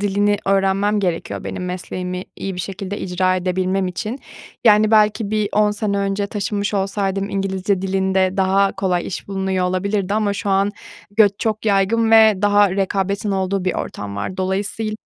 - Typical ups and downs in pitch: No, narrow, 1.5 semitones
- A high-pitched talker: Yes, high, 195 Hz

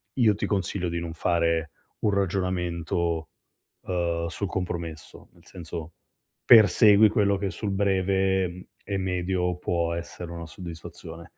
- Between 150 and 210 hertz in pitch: No, very low, 90 Hz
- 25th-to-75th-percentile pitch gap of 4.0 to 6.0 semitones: No, narrow, 2.5 semitones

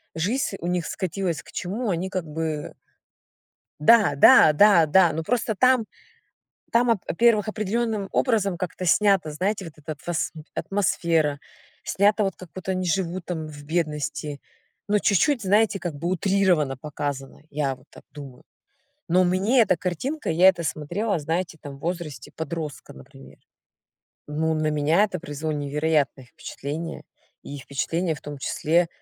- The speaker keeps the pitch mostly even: No, average, 4.6 semitones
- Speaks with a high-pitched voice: No, medium, 170 Hz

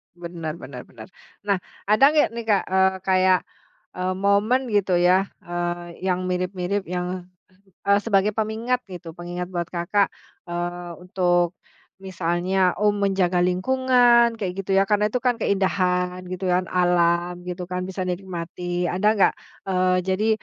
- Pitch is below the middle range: No, medium, 185 Hz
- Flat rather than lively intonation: Yes, narrow, 2.2 semitones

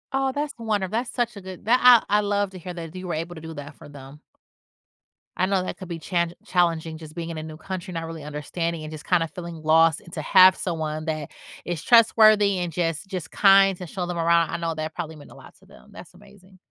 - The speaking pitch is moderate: Yes, medium, 175 Hz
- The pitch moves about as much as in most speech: Yes, average, 3.4 semitones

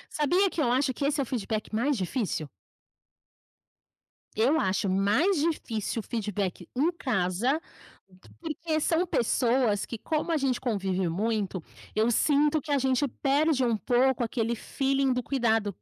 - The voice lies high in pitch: Yes, very high, 250 Hz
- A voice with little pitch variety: No, average, 5.1 semitones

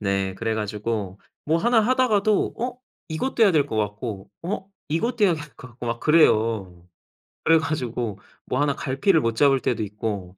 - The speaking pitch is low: Yes, low, 130 Hz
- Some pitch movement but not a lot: No, wide, 8.0 semitones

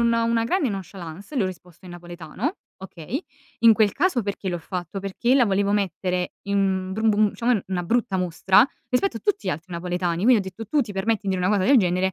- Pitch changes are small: No, average, 4.2 semitones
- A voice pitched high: Yes, high, 195 Hz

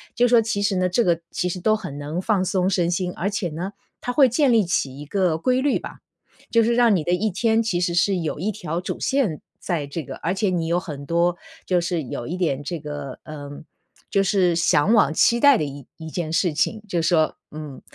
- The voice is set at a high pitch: No, medium, 180 Hz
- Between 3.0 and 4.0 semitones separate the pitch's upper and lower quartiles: No, average, 4.7 semitones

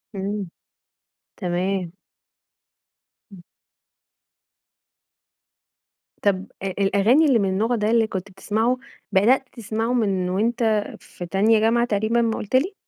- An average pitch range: Yes, average, 3.3 semitones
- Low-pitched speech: No, high, 210 Hz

